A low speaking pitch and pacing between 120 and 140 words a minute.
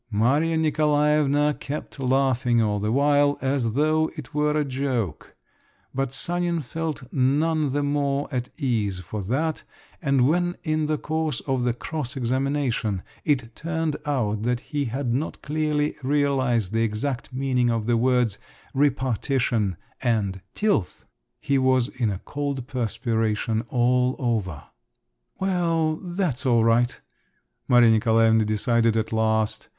Yes: low, 130 Hz; slow, 135 wpm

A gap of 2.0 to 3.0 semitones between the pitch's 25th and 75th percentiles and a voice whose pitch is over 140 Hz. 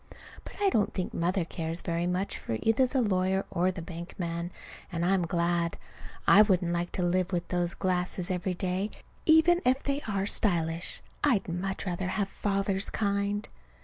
Yes: narrow, 2.6 semitones; medium, 185 Hz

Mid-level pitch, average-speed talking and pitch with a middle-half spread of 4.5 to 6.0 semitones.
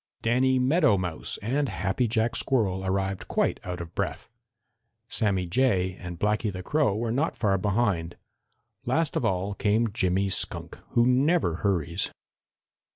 No: low, 105 Hz; average, 145 wpm; average, 4.8 semitones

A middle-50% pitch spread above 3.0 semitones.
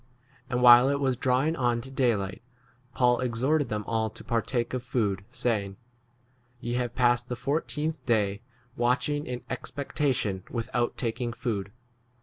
No: narrow, 2.4 semitones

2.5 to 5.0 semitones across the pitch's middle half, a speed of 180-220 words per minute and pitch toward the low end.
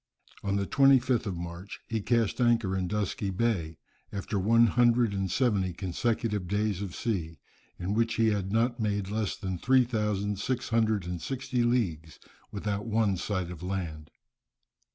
No: average, 3.7 semitones; average, 160 wpm; low, 105 Hz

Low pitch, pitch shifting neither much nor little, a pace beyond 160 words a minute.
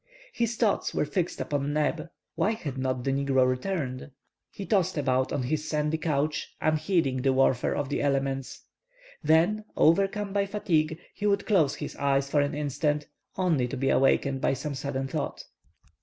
No: medium, 150 Hz; average, 3.8 semitones; average, 170 wpm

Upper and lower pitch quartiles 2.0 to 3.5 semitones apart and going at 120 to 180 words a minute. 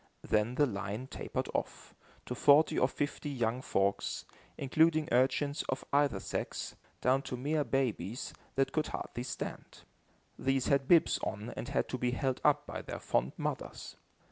Yes: average, 3.1 semitones; average, 160 wpm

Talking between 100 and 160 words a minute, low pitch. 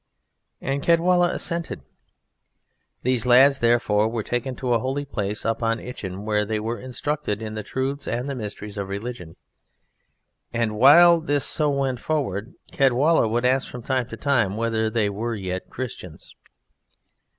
Yes: average, 155 wpm; low, 120 Hz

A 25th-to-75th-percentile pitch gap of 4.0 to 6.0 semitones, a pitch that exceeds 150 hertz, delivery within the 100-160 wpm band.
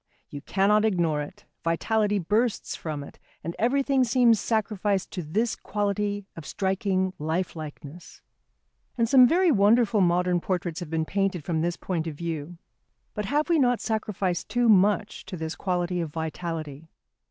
Yes: average, 4.5 semitones; high, 190 Hz; average, 155 wpm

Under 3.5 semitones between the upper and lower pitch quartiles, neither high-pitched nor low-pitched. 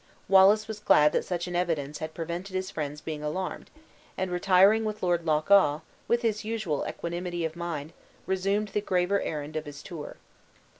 No: average, 3.9 semitones; medium, 175 Hz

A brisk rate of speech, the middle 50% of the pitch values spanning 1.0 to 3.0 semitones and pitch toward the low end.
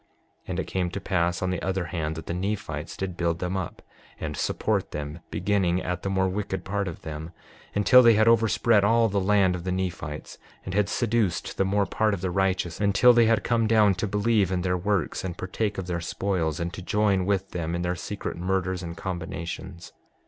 Yes: fast, 215 wpm; average, 2.7 semitones; very low, 95 Hz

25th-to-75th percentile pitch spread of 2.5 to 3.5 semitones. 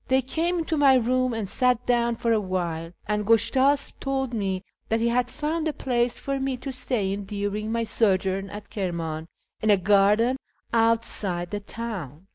No: average, 4.4 semitones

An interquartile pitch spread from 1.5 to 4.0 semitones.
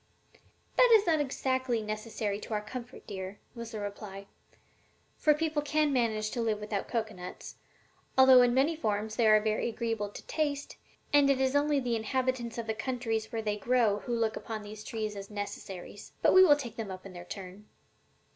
Yes: average, 3.7 semitones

